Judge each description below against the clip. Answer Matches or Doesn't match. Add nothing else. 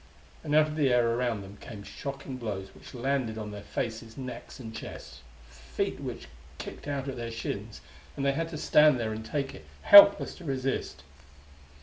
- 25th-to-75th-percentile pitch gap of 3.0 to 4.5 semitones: Matches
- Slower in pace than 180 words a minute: Doesn't match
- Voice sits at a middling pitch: Doesn't match